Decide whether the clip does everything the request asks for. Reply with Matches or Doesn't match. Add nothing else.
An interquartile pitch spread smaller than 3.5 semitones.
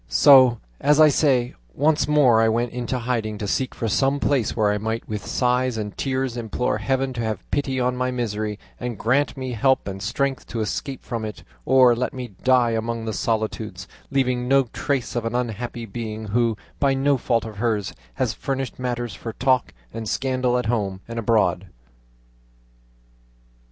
Matches